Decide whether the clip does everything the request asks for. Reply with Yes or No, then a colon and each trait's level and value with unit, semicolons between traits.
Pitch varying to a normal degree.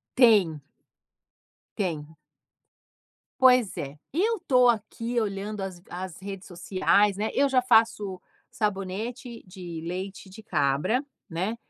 Yes: average, 4.1 semitones